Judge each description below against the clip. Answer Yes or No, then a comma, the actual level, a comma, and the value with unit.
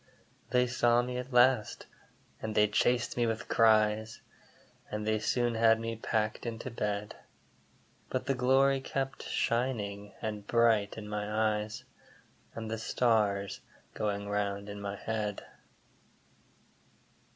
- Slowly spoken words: Yes, slow, 130 wpm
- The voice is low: Yes, low, 110 Hz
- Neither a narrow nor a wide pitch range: No, narrow, 2.3 semitones